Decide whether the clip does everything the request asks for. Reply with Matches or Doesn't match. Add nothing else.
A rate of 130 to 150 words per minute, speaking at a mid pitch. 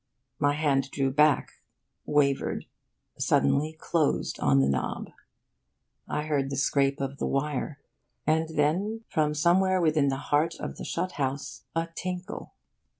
Matches